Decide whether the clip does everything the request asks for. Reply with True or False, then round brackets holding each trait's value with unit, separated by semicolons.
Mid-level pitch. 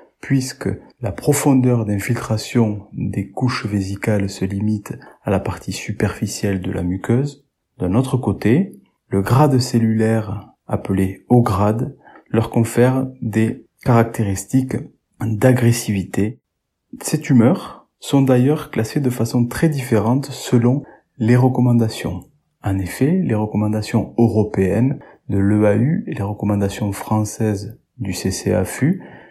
False (110 Hz)